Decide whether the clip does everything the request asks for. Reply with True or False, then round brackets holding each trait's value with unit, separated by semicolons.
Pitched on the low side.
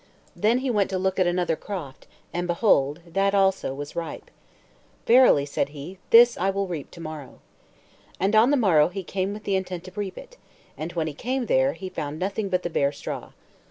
False (185 Hz)